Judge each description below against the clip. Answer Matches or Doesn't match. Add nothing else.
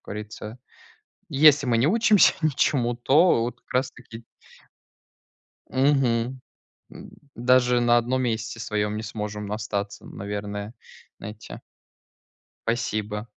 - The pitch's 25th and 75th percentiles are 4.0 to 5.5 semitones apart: Doesn't match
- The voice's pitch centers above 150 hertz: Doesn't match